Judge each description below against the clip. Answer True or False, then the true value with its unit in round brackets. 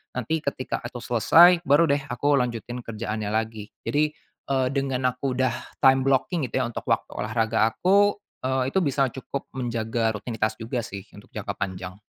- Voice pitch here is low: True (125 Hz)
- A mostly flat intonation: False (3.6 semitones)